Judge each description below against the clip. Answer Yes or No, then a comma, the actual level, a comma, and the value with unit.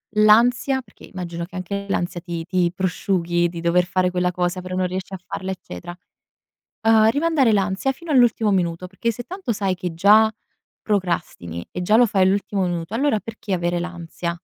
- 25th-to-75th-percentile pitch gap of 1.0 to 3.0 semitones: No, average, 3.7 semitones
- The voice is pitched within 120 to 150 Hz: No, medium, 185 Hz